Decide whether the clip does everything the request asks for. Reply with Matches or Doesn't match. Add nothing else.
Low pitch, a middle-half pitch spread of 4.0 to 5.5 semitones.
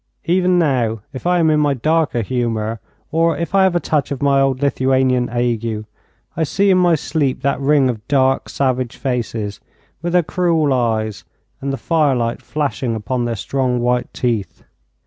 Matches